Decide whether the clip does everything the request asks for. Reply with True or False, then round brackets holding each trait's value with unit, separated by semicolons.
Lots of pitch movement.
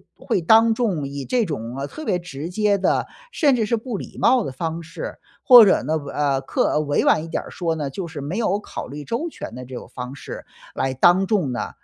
True (7.7 semitones)